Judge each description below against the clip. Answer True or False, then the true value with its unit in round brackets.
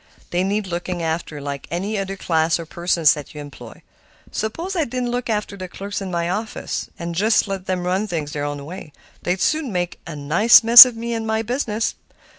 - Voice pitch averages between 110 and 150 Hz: False (185 Hz)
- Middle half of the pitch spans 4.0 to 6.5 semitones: True (4.8 semitones)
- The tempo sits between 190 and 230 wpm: True (205 wpm)